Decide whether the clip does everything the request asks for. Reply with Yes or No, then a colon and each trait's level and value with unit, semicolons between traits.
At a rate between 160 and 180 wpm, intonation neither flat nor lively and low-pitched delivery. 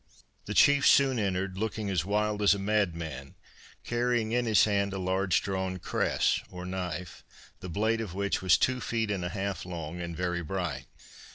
Yes: average, 175 wpm; average, 3.1 semitones; very low, 95 Hz